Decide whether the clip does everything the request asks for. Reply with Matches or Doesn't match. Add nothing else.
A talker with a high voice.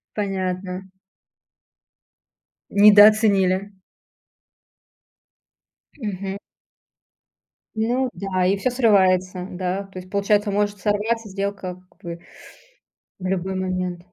Matches